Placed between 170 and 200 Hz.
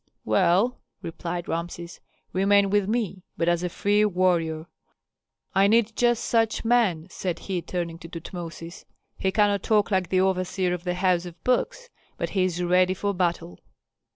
Yes: medium, 185 Hz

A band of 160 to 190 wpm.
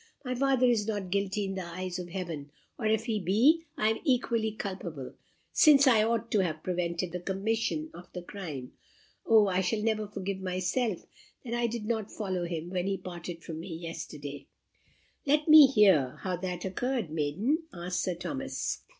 Yes: average, 180 wpm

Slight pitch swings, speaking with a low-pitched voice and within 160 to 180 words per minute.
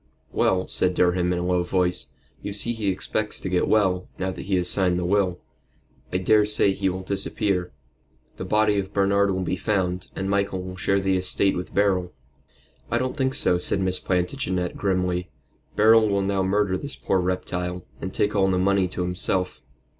No: narrow, 1.6 semitones; very low, 95 Hz; average, 190 wpm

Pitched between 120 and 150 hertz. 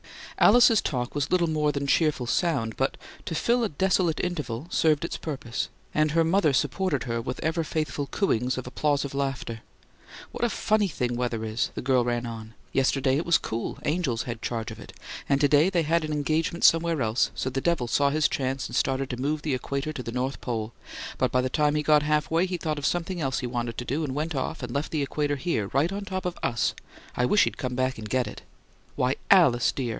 Yes: medium, 140 Hz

